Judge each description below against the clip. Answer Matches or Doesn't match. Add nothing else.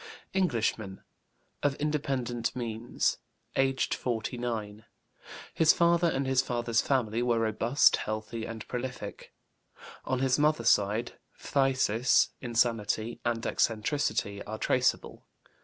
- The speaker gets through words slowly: Matches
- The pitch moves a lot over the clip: Doesn't match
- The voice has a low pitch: Matches